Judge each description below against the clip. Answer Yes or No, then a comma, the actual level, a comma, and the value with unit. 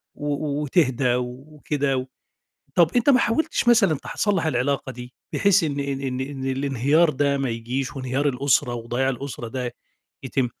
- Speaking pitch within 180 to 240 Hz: No, low, 135 Hz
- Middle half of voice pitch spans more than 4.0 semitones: No, average, 2.8 semitones